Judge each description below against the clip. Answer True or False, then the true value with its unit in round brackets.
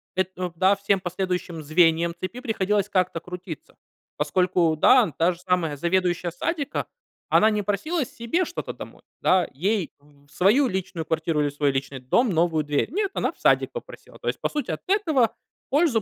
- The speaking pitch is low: False (185 Hz)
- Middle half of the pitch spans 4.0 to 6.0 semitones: True (5.3 semitones)